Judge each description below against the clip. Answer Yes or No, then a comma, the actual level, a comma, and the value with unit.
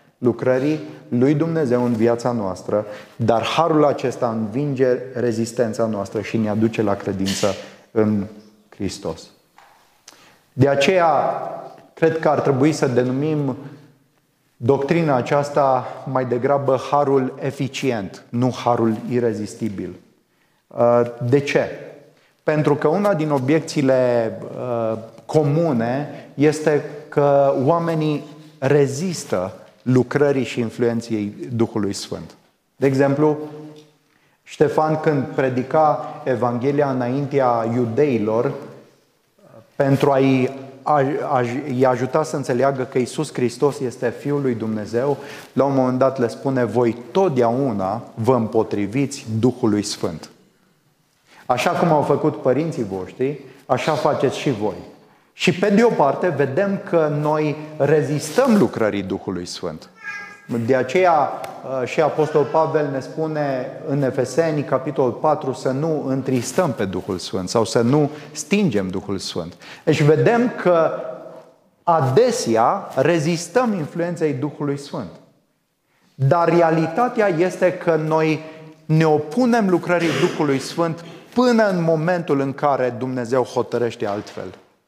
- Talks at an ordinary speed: No, slow, 110 wpm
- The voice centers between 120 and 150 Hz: Yes, medium, 140 Hz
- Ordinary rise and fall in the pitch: Yes, average, 4.1 semitones